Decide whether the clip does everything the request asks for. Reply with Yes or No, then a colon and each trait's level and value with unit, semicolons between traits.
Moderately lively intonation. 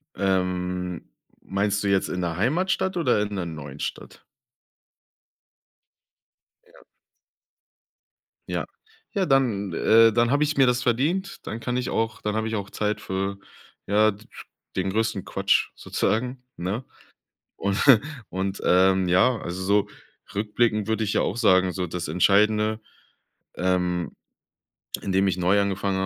Yes: average, 3.5 semitones